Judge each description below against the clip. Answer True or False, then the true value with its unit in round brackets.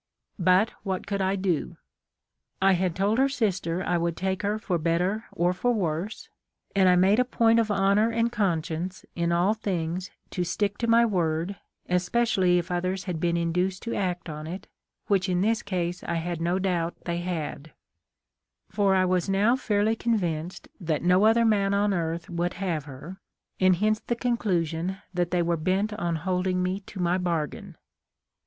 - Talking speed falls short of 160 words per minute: False (180 wpm)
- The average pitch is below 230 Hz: True (185 Hz)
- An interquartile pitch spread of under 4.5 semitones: True (2.9 semitones)